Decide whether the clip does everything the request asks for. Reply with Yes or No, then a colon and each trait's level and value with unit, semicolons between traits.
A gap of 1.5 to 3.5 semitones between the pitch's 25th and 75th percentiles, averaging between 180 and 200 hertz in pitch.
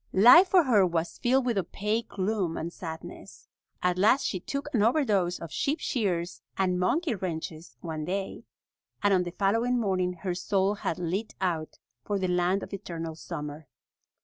No: average, 4.1 semitones; high, 190 Hz